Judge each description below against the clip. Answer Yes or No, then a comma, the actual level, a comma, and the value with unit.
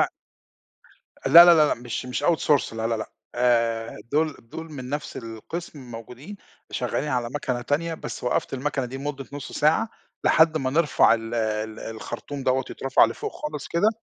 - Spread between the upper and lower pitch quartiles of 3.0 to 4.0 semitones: No, average, 4.5 semitones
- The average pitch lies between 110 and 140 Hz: Yes, low, 135 Hz